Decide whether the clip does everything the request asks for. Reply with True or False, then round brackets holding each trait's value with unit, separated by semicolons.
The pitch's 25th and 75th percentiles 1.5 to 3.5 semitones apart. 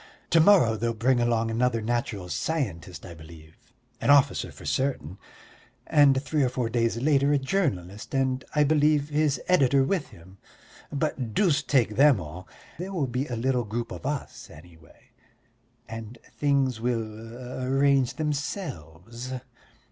False (4.3 semitones)